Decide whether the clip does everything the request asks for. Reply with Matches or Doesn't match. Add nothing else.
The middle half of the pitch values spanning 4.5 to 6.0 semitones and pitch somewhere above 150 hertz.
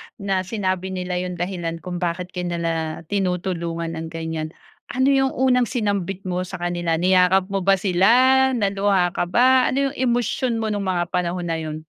Doesn't match